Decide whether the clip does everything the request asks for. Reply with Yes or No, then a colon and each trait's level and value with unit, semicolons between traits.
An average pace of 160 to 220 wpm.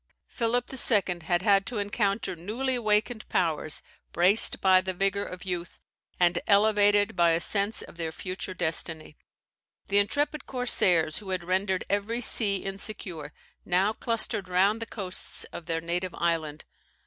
No: average, 150 wpm